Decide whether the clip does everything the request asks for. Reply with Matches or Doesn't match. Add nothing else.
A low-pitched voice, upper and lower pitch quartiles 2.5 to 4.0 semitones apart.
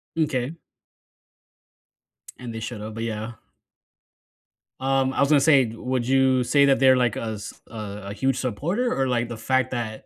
Matches